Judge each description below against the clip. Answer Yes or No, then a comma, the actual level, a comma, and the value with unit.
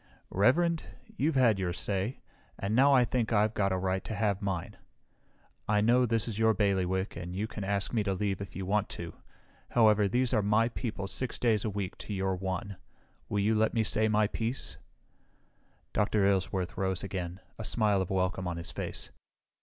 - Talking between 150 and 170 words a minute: No, average, 195 wpm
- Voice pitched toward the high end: No, low, 105 Hz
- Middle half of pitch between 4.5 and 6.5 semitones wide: No, average, 2.8 semitones